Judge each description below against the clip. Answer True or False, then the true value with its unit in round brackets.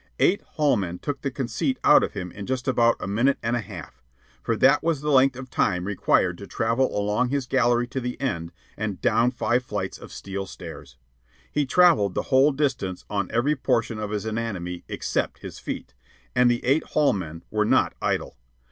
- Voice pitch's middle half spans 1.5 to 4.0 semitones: False (4.7 semitones)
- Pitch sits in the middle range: False (120 Hz)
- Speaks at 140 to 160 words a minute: False (200 wpm)